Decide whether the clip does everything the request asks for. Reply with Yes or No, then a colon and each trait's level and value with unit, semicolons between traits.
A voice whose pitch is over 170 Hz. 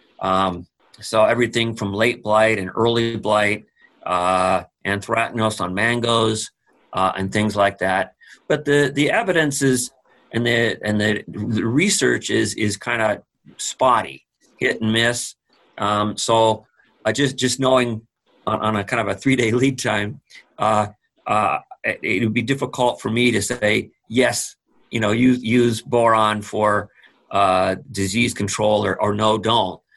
No: low, 110 Hz